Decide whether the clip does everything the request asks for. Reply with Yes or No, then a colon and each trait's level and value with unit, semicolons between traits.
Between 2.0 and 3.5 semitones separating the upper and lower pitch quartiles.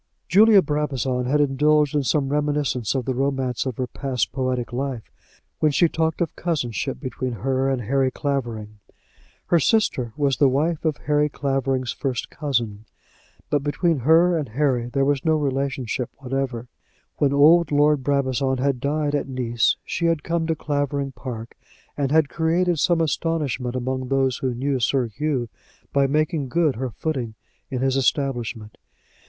Yes: average, 2.7 semitones